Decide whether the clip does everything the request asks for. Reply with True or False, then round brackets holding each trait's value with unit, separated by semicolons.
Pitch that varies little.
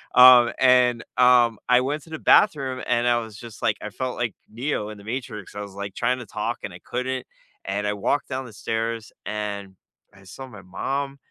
False (3.4 semitones)